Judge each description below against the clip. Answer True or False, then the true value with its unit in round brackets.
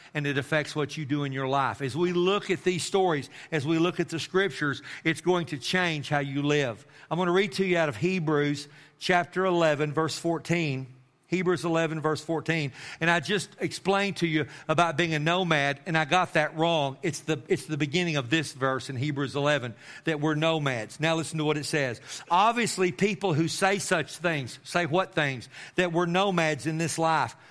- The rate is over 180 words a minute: True (205 wpm)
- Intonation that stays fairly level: False (3.3 semitones)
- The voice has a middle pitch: True (160 Hz)